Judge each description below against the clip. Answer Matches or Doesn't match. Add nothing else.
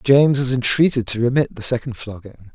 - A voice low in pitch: Matches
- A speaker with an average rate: Matches